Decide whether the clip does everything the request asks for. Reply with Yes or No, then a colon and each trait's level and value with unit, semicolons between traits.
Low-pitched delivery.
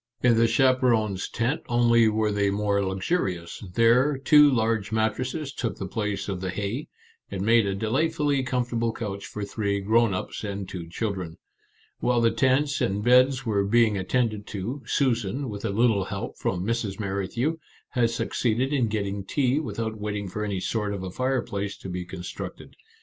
Yes: low, 110 Hz